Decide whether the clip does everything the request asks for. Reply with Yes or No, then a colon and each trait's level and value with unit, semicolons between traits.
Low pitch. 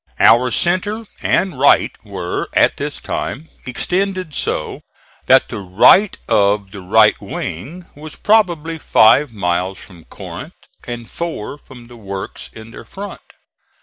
Yes: low, 125 Hz